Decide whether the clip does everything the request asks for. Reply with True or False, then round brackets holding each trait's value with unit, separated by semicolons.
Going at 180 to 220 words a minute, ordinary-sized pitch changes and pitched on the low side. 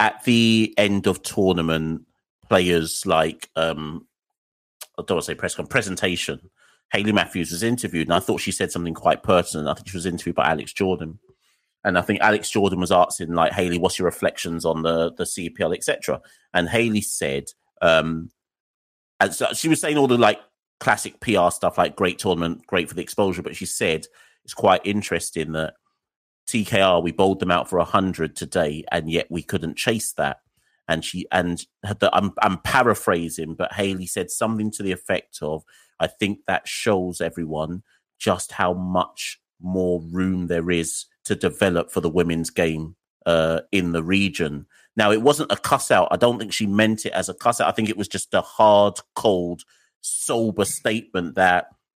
True (185 wpm; 3.7 semitones; 90 Hz)